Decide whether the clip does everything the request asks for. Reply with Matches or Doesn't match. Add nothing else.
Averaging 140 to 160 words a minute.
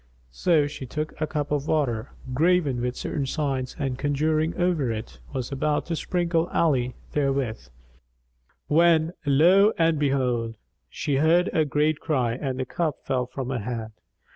Matches